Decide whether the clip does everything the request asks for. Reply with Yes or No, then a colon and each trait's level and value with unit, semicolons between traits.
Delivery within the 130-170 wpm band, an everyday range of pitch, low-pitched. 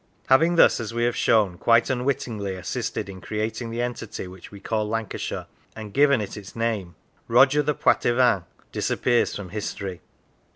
Yes: average, 160 wpm; average, 3.4 semitones; low, 115 Hz